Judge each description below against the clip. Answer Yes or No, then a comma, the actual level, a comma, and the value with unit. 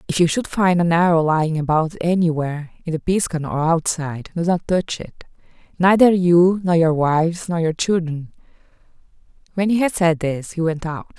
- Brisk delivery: No, average, 180 wpm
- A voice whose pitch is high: No, medium, 170 Hz